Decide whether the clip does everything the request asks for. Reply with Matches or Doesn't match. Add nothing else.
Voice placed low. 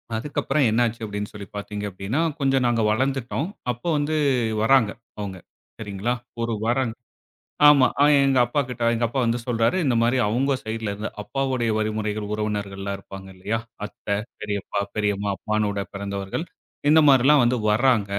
Matches